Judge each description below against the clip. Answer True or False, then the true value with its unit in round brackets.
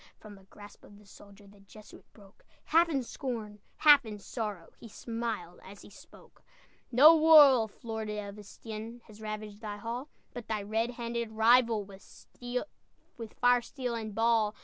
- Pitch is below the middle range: False (220 Hz)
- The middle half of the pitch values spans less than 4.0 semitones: True (2.7 semitones)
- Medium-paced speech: True (160 wpm)